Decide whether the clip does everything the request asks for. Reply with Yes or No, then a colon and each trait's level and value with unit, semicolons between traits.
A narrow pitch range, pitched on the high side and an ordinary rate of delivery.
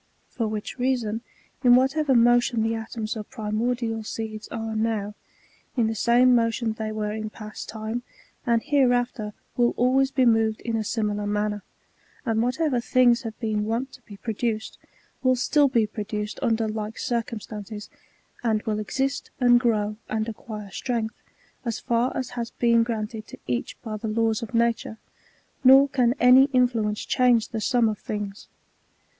Yes: narrow, 2.2 semitones; high, 225 Hz; average, 160 wpm